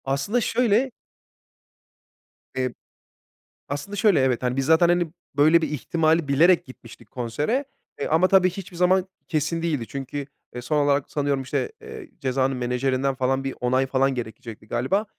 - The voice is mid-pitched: Yes, medium, 145 Hz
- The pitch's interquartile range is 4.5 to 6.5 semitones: Yes, average, 5.1 semitones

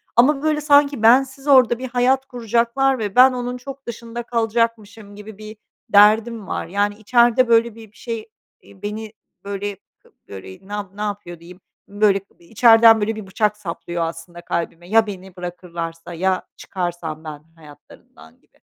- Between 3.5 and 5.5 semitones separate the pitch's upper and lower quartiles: Yes, average, 4.3 semitones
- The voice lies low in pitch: No, high, 215 Hz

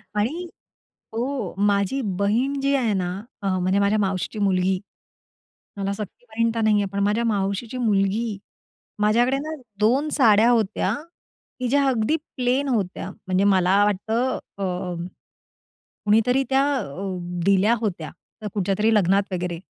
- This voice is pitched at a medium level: No, high, 210 Hz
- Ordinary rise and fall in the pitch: Yes, average, 3.7 semitones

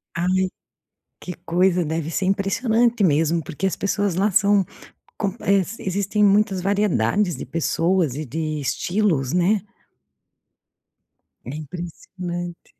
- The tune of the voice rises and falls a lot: No, average, 3.3 semitones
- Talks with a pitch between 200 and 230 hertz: No, medium, 185 Hz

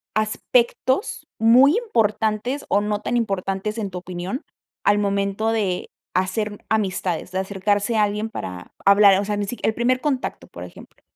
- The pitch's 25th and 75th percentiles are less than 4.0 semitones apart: Yes, narrow, 2.6 semitones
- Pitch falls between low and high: No, high, 210 Hz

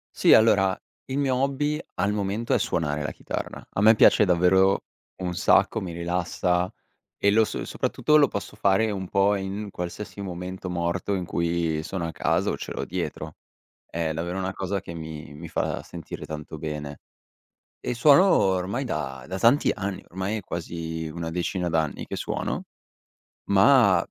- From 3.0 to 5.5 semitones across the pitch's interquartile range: Yes, average, 3.3 semitones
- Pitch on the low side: Yes, very low, 95 Hz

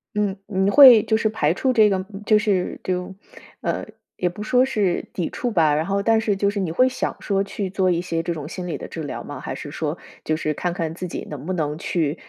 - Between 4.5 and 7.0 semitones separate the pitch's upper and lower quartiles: No, average, 4.0 semitones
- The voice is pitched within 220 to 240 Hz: No, high, 190 Hz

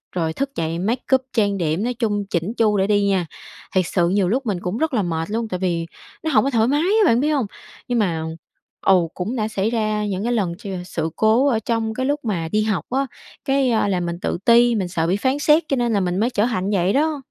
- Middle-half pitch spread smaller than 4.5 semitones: No, average, 5.0 semitones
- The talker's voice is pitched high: Yes, high, 215 Hz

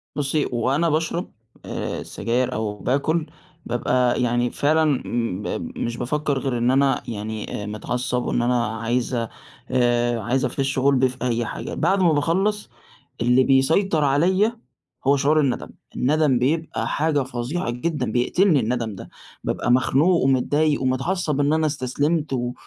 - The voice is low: Yes, low, 130 Hz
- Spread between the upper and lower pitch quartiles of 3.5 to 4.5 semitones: Yes, average, 4.0 semitones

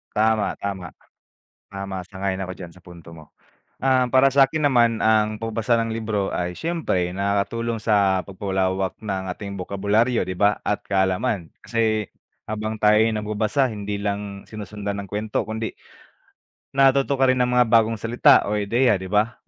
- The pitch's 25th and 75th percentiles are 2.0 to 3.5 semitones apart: Yes, average, 2.8 semitones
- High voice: No, low, 105 Hz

